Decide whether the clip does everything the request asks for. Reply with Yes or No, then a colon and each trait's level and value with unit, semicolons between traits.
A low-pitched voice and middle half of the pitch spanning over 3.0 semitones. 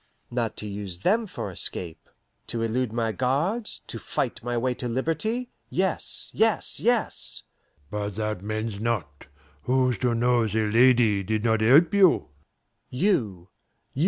Yes: low, 115 Hz; average, 4.3 semitones